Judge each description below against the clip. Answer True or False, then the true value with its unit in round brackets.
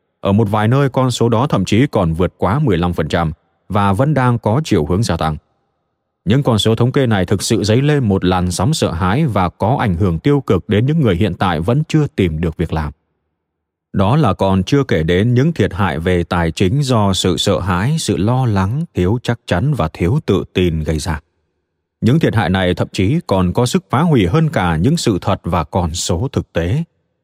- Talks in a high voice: False (100 Hz)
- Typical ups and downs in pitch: False (6.0 semitones)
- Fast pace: False (225 wpm)